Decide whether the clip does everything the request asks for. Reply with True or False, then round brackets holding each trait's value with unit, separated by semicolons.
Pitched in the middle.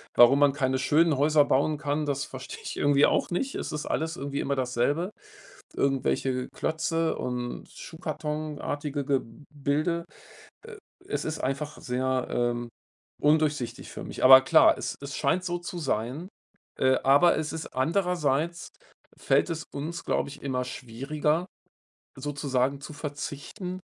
True (145 Hz)